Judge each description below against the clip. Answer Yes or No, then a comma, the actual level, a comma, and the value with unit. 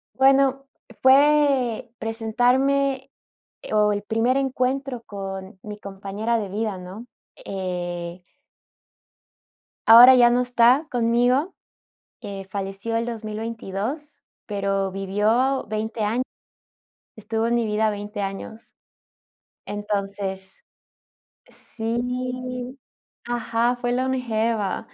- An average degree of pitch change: Yes, average, 3.7 semitones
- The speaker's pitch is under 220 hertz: No, high, 225 Hz